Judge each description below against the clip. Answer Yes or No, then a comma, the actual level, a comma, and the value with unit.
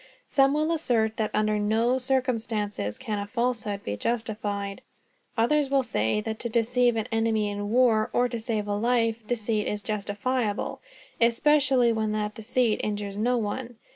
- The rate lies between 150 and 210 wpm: Yes, average, 155 wpm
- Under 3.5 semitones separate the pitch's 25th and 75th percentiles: Yes, average, 2.8 semitones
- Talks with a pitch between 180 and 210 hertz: No, high, 225 Hz